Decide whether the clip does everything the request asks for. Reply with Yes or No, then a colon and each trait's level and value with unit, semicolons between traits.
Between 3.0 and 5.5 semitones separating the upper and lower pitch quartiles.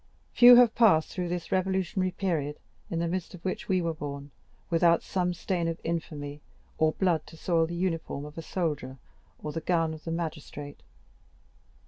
No: narrow, 2.6 semitones